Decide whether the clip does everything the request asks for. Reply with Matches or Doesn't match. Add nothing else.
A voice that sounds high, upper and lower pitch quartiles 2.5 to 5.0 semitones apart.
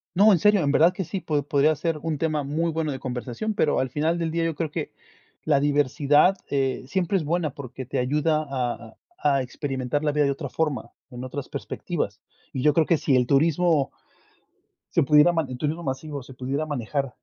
Doesn't match